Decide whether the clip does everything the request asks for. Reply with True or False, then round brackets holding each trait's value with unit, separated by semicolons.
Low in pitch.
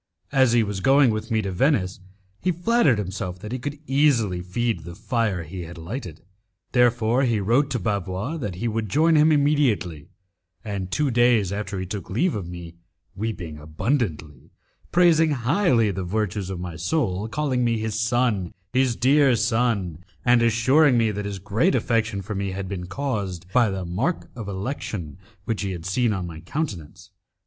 True (110 Hz)